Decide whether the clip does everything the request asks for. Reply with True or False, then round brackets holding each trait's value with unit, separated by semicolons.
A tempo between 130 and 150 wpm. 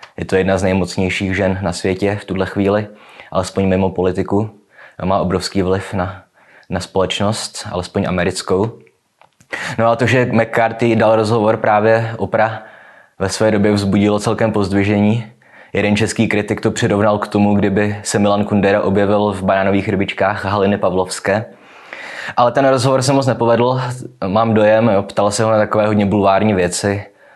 False (160 wpm)